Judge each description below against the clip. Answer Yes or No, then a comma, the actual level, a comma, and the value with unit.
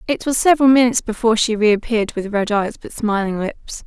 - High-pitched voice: Yes, high, 225 Hz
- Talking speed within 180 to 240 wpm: Yes, average, 200 wpm